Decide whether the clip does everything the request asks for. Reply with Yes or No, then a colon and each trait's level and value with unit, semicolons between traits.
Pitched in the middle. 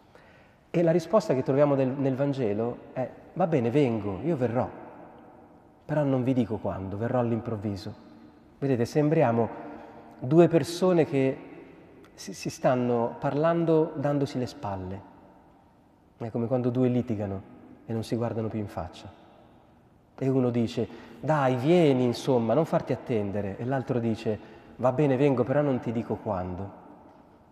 No: low, 125 Hz